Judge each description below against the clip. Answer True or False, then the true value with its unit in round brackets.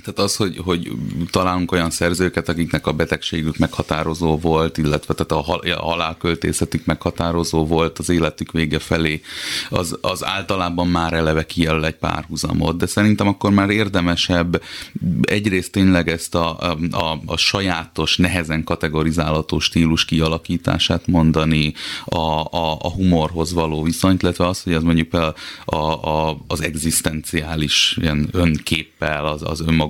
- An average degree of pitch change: False (1.7 semitones)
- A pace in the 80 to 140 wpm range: True (135 wpm)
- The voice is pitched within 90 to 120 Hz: False (80 Hz)